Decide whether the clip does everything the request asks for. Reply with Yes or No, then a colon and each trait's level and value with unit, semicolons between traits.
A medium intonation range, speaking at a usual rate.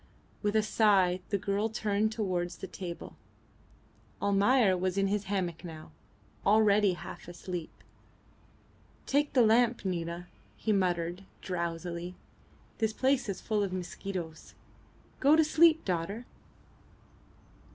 No: average, 3.5 semitones; slow, 120 wpm